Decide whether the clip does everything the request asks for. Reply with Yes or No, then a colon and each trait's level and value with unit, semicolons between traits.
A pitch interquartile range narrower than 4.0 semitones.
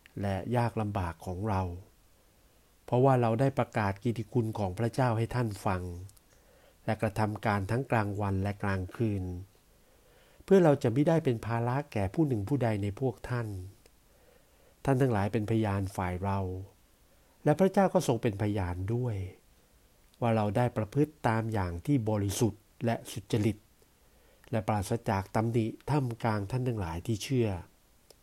Yes: average, 3.6 semitones